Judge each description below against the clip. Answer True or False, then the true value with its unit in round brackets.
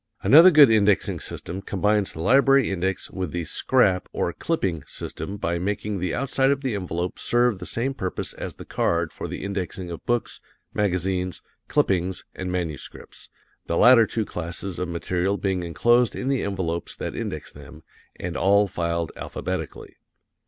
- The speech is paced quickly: False (160 wpm)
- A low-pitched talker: True (95 Hz)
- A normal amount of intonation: True (4.3 semitones)